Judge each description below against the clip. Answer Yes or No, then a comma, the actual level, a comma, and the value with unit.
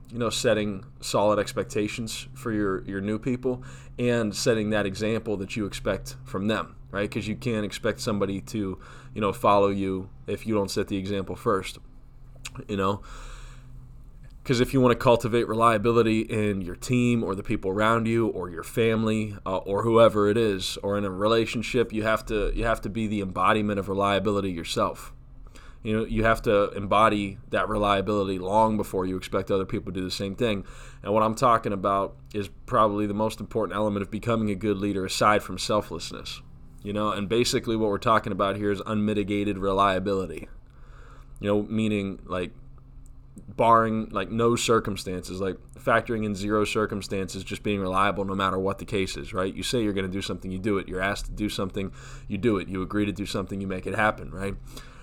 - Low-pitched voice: Yes, low, 105 Hz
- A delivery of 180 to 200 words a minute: Yes, average, 195 wpm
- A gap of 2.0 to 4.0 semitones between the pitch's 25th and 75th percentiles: Yes, narrow, 2.5 semitones